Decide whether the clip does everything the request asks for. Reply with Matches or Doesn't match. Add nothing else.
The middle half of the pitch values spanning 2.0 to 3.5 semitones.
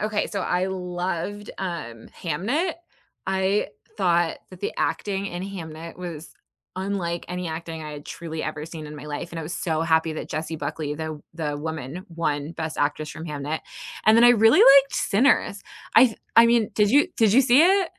Doesn't match